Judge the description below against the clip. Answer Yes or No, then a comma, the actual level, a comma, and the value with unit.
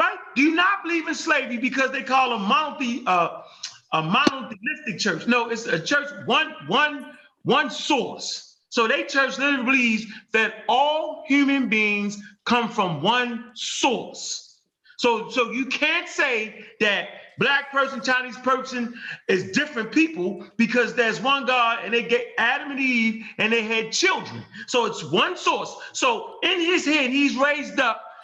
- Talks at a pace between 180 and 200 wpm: No, average, 155 wpm